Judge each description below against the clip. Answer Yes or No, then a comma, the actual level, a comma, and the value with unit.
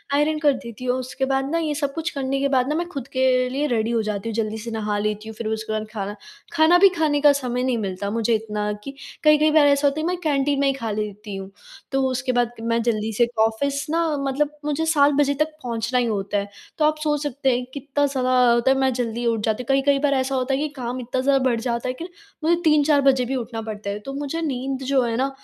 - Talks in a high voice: Yes, very high, 260 Hz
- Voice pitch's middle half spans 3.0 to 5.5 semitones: Yes, average, 3.9 semitones